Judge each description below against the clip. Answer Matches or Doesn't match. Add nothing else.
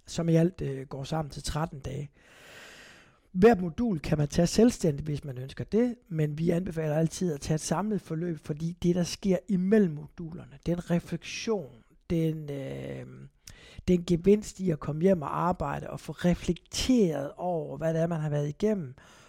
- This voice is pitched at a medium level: Matches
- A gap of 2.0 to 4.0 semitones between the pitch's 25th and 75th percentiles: Matches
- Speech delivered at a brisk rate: Doesn't match